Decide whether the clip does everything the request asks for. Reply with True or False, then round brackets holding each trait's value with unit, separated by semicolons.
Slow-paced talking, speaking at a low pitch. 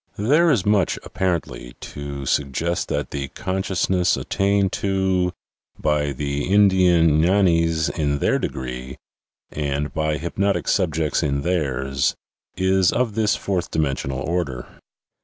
True (120 wpm; 85 Hz)